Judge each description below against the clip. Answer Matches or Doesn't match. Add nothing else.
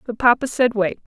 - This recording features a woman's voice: Matches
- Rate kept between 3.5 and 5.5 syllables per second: Matches